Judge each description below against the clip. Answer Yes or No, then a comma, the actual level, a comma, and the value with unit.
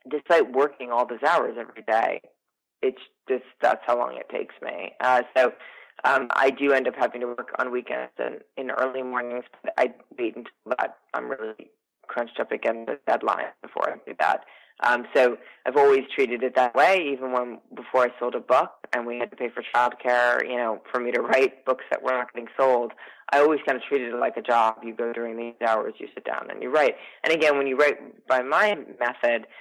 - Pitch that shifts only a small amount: Yes, narrow, 2.1 semitones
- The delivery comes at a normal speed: No, fast, 220 wpm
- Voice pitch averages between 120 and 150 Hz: Yes, low, 125 Hz